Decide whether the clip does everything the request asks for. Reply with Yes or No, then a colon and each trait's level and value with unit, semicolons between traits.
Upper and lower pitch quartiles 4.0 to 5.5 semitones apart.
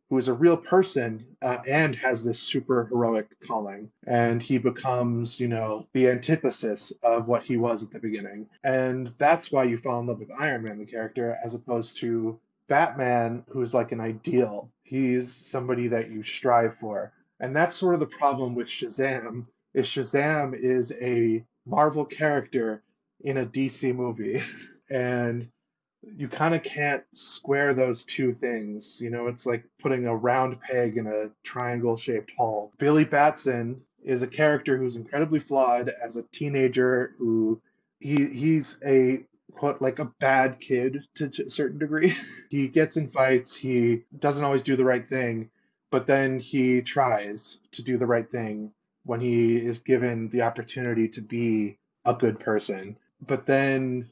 No: narrow, 2.5 semitones